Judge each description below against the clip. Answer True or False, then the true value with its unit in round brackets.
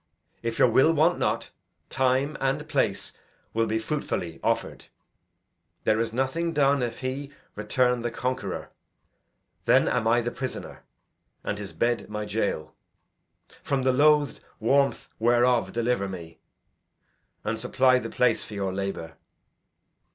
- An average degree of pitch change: True (3.3 semitones)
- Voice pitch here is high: False (120 Hz)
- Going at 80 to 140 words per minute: True (135 wpm)